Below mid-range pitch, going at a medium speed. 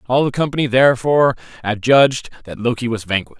Yes: low, 125 Hz; average, 160 wpm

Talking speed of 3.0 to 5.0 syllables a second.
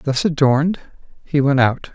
Yes: 4.5 syllables/s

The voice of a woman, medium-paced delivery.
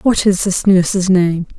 Yes: female; average, 190 wpm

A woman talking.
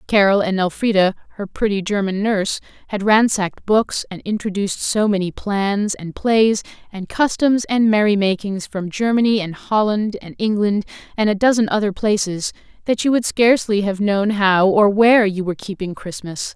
Yes: female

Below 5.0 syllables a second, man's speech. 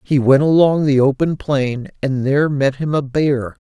Yes: 4.5 syllables/s; male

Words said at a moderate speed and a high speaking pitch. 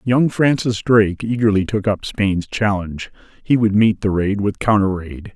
No: average, 180 wpm; low, 105 Hz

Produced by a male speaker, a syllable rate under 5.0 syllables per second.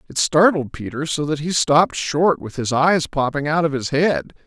Yes: male; 4.8 syllables/s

